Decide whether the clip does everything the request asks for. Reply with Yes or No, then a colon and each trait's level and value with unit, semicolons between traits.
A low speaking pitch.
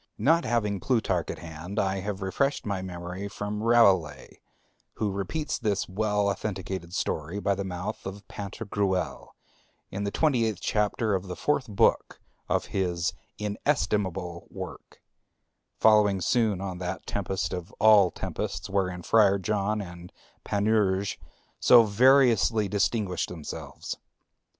Yes: low, 100 Hz